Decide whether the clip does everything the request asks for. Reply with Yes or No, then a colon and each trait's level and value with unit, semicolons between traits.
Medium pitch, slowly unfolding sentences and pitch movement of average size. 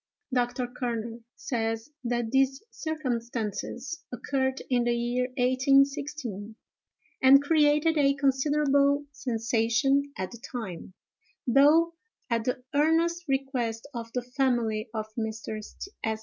No: very high, 255 Hz; slow, 110 wpm; average, 3.5 semitones